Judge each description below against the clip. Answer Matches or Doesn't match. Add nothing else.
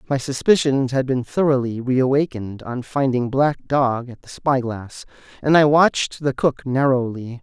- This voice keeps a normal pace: Matches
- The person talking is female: Doesn't match